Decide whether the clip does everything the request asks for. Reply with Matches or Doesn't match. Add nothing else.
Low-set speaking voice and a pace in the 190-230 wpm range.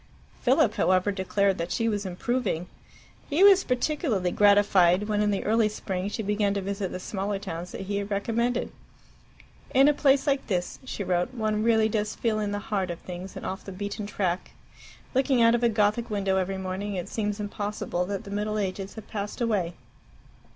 Doesn't match